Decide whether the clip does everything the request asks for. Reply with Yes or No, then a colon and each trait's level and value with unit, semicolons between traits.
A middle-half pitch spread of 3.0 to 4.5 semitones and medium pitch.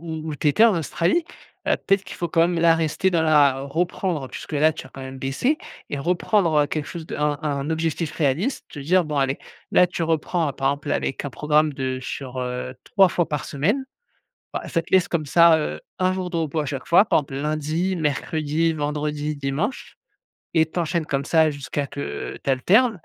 Yes: average, 3.3 semitones; medium, 155 Hz